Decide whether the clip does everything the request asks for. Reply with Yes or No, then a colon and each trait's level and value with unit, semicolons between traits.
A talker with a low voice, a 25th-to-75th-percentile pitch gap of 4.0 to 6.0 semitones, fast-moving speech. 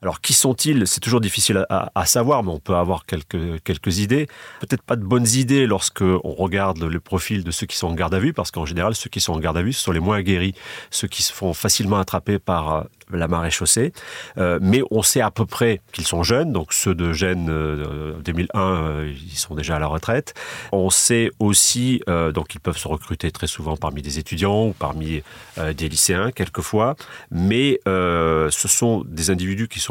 Yes: very low, 95 Hz; average, 4.5 semitones; fast, 225 wpm